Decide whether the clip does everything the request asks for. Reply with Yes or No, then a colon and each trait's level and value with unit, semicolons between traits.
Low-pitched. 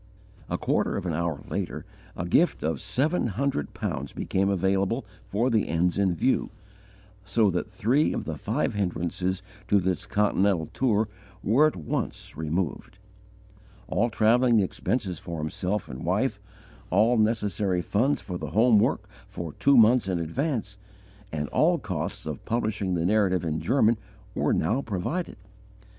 Yes: low, 100 Hz